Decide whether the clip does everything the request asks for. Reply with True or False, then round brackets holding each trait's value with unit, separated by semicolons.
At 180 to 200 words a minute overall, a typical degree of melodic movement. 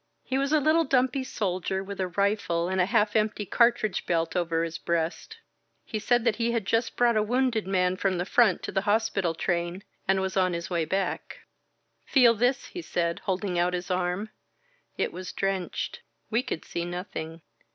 True (190 wpm; 4.5 semitones)